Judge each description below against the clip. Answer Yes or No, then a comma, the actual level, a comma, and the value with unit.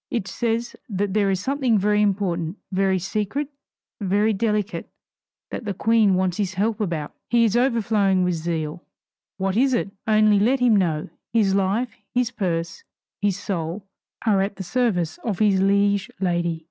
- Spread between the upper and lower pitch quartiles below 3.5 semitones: Yes, average, 3.0 semitones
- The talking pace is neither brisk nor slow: Yes, average, 160 wpm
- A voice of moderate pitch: No, high, 200 Hz